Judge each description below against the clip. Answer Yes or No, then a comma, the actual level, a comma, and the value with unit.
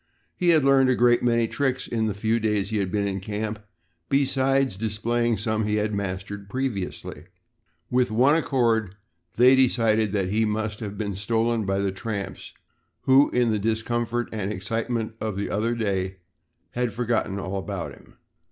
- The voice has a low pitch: Yes, low, 110 Hz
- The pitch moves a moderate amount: Yes, average, 3.0 semitones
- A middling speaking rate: Yes, average, 170 wpm